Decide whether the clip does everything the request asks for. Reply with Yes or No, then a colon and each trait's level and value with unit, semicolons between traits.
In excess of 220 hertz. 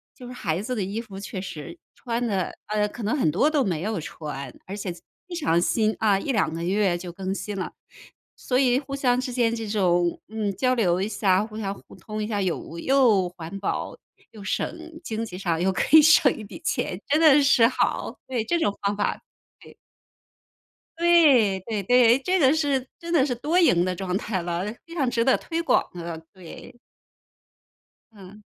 No: high, 215 Hz